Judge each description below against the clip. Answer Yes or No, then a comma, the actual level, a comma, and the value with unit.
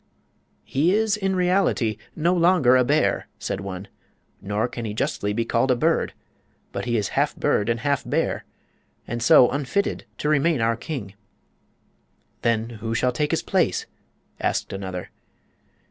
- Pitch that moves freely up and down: Yes, wide, 5.8 semitones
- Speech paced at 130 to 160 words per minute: Yes, average, 155 wpm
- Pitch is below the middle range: Yes, low, 125 Hz